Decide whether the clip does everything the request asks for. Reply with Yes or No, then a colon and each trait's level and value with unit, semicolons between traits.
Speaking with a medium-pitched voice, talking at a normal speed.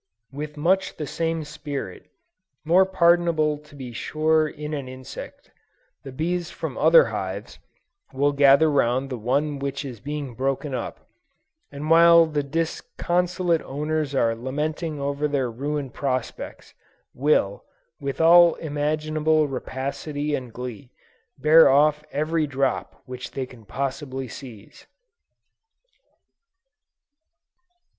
No: medium, 145 Hz; slow, 120 wpm